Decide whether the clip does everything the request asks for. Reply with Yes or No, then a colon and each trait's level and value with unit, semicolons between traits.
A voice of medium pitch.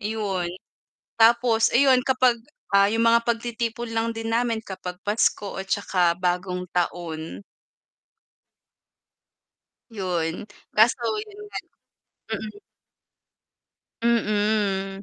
No: high, 215 Hz